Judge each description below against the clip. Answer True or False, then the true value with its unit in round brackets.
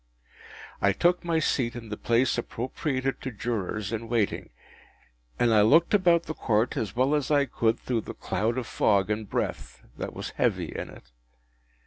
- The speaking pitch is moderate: False (120 Hz)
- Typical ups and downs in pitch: True (4.4 semitones)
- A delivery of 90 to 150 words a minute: False (175 wpm)